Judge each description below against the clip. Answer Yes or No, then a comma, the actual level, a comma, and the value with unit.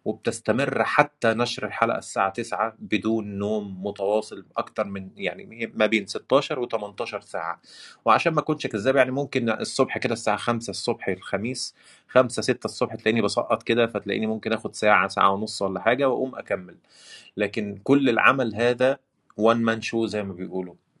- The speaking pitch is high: No, low, 110 Hz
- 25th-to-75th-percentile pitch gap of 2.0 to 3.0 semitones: Yes, narrow, 2.6 semitones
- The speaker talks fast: Yes, fast, 160 wpm